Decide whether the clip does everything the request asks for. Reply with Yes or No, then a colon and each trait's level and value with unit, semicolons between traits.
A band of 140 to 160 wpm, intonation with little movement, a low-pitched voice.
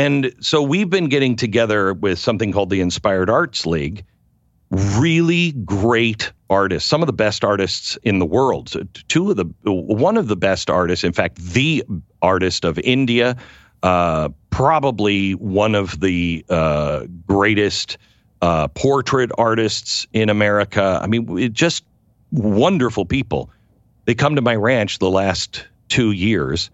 No: average, 145 wpm; average, 4.5 semitones; low, 105 Hz